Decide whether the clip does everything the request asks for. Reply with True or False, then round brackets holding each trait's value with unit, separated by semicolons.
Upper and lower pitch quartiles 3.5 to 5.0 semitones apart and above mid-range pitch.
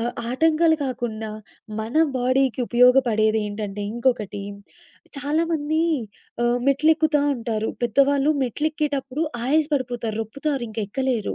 True (4.4 semitones; 255 Hz)